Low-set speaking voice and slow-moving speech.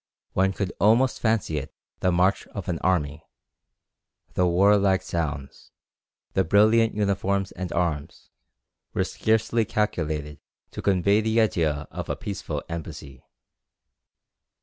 Yes: very low, 95 Hz; slow, 120 wpm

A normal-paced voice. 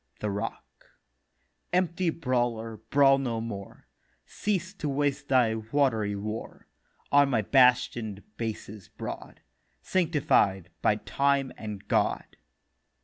No: slow, 105 wpm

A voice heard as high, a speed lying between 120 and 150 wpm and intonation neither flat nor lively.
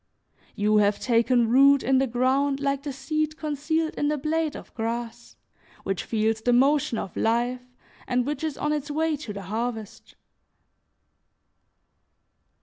Yes: very high, 260 Hz; average, 145 wpm; average, 4.3 semitones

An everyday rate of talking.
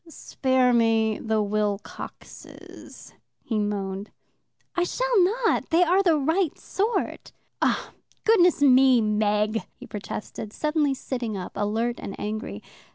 No: slow, 120 wpm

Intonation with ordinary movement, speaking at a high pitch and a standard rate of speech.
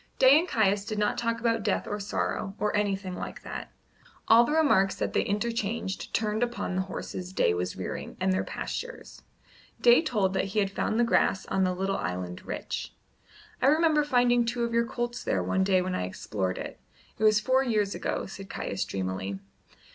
Yes: average, 3.9 semitones; high, 210 Hz; average, 195 wpm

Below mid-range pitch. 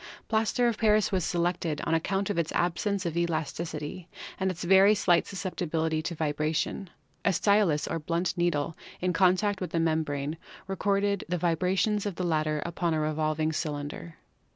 No: medium, 170 Hz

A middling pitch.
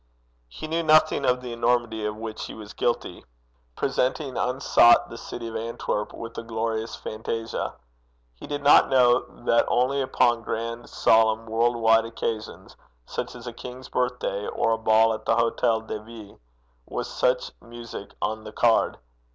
No: low, 115 Hz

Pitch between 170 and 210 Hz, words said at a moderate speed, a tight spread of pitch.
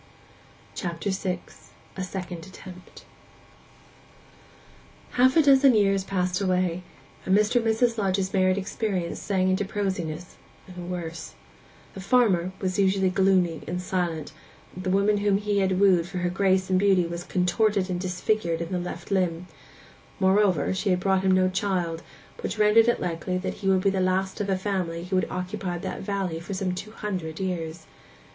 Yes: medium, 185 Hz; average, 165 wpm; narrow, 1.8 semitones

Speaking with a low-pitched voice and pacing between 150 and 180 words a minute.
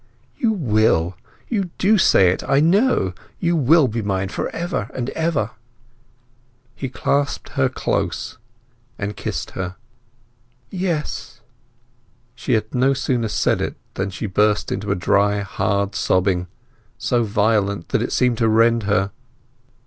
No: low, 110 Hz; slow, 135 wpm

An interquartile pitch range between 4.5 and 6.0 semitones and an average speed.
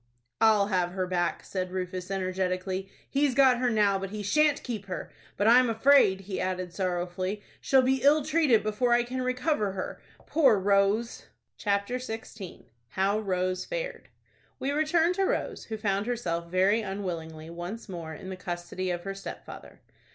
Yes: average, 5.0 semitones; average, 165 wpm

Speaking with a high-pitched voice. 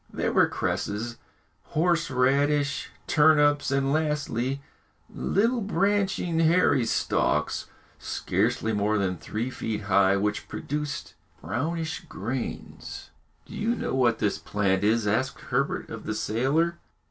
No: low, 135 Hz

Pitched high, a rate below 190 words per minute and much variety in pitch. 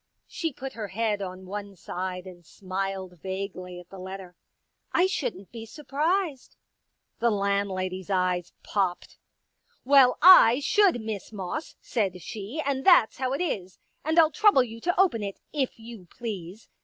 Yes: high, 210 Hz; average, 165 wpm; wide, 6.4 semitones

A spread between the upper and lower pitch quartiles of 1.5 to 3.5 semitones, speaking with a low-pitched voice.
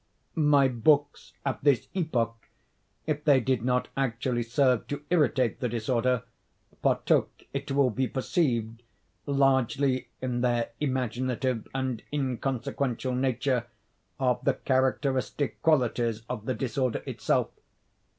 Yes: narrow, 2.4 semitones; low, 130 Hz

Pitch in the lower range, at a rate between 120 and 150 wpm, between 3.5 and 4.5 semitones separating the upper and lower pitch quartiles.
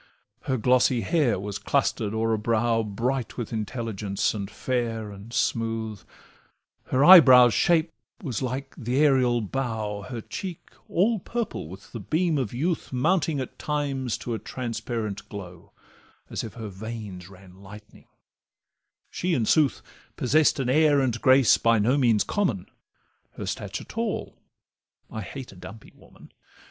Yes: low, 120 Hz; average, 145 wpm; average, 4.2 semitones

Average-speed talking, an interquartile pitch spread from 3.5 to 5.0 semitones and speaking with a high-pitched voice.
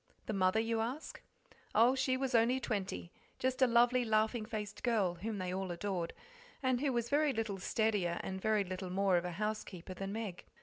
Yes: average, 190 wpm; average, 4.1 semitones; high, 215 Hz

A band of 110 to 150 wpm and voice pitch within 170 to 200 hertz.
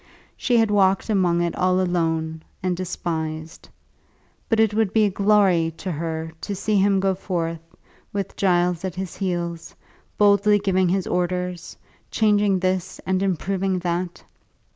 Yes: average, 145 wpm; medium, 185 Hz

